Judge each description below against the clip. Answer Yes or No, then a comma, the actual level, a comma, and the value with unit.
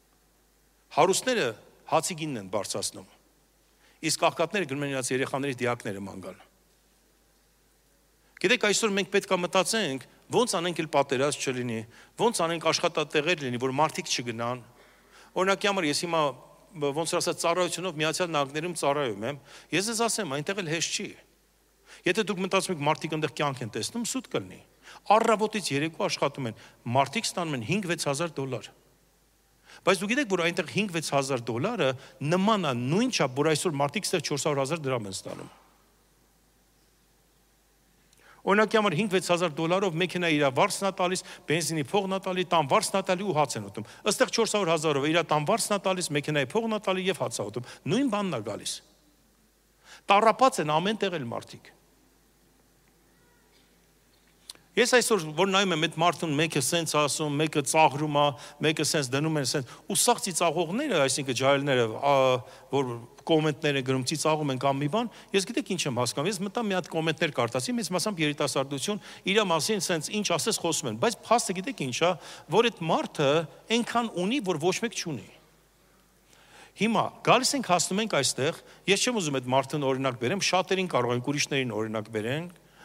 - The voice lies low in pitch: No, medium, 165 Hz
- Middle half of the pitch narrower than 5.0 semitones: No, wide, 5.5 semitones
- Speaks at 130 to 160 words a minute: Yes, average, 155 wpm